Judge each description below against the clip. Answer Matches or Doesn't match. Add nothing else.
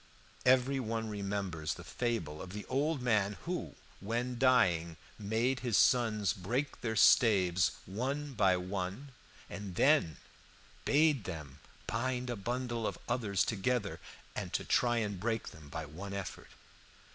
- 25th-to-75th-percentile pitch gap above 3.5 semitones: Matches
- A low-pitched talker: Matches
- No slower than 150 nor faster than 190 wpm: Doesn't match